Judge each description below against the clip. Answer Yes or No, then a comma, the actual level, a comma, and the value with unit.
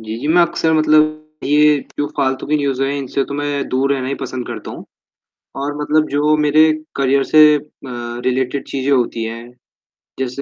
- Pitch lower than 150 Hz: Yes, medium, 140 Hz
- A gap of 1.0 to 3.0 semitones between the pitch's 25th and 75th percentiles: Yes, narrow, 2.6 semitones